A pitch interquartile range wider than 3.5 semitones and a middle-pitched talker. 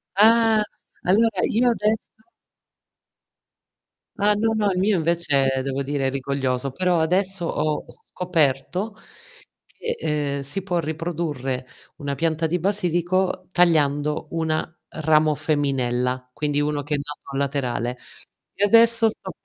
Yes: average, 5.3 semitones; medium, 160 Hz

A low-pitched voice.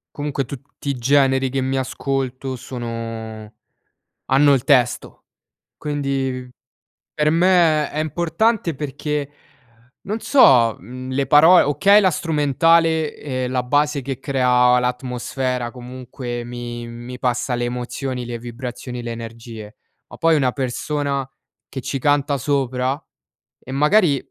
Yes: low, 130 Hz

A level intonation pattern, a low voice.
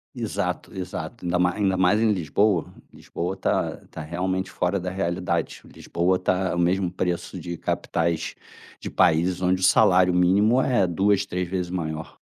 Yes: narrow, 1.4 semitones; very low, 90 Hz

